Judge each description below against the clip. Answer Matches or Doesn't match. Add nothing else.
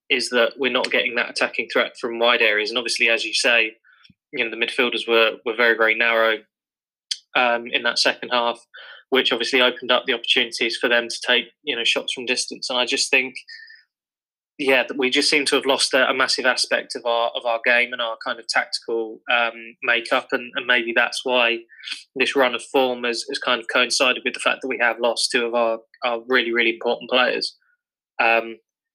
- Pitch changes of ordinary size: Doesn't match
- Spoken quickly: Matches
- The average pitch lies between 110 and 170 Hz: Matches